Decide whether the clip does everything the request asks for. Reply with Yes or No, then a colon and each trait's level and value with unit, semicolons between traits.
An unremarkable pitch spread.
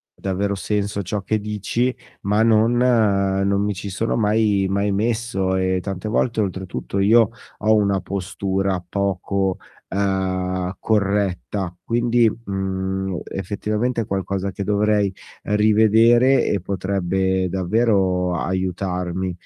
No: narrow, 2.2 semitones